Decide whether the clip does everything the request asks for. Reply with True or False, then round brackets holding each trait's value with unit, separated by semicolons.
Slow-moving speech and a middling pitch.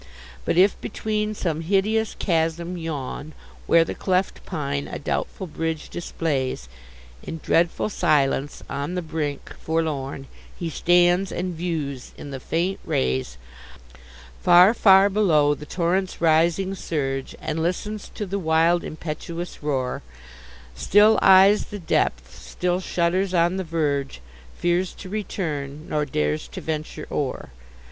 True (130 wpm; 165 Hz)